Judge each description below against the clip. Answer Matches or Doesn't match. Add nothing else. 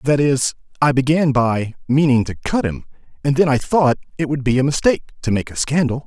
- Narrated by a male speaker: Matches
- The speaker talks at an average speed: Doesn't match